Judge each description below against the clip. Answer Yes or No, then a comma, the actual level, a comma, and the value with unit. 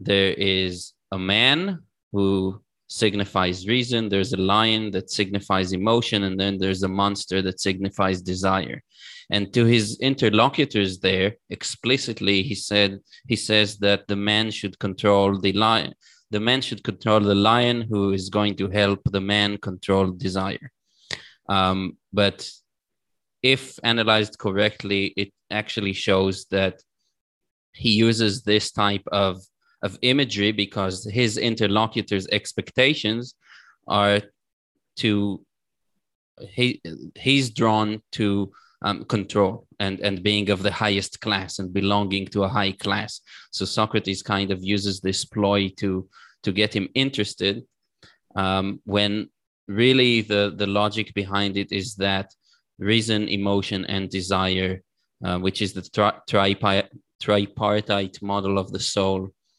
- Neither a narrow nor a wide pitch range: No, narrow, 1.9 semitones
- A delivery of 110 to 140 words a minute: Yes, slow, 135 wpm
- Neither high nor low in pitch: No, low, 100 Hz